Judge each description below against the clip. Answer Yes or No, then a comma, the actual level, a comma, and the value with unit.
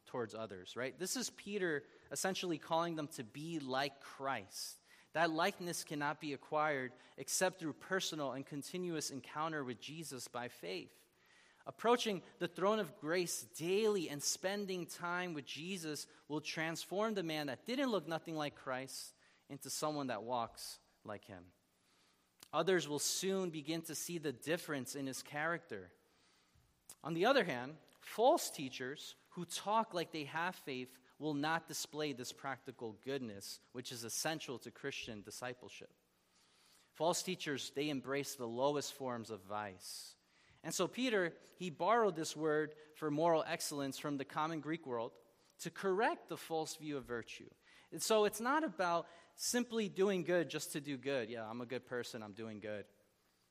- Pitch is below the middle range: No, medium, 150 Hz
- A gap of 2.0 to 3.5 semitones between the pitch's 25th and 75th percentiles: No, average, 5.2 semitones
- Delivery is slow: No, average, 160 wpm